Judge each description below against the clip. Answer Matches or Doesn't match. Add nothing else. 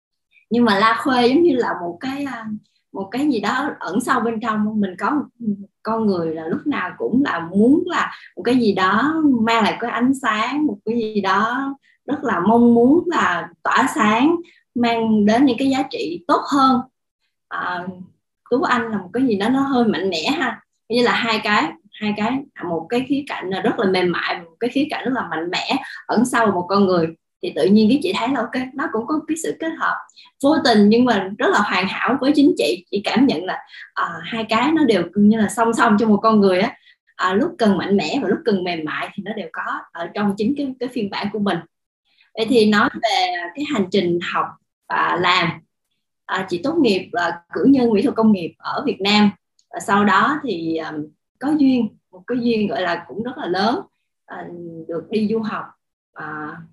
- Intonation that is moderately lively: Matches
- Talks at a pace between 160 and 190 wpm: Doesn't match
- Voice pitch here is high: Matches